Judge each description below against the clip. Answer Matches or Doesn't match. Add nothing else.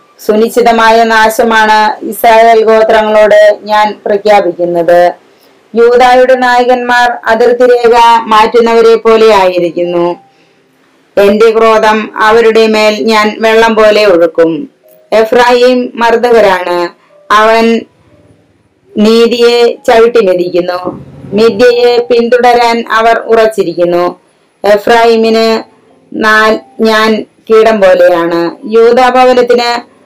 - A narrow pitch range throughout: Matches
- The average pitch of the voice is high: Matches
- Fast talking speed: Doesn't match